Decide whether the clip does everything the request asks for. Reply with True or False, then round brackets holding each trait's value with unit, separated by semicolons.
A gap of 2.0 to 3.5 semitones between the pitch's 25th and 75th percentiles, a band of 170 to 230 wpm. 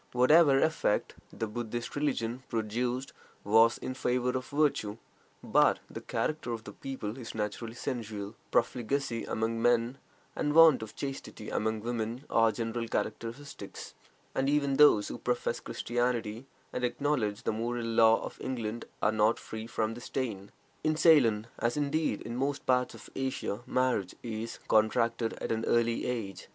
False (2.9 semitones; 150 wpm)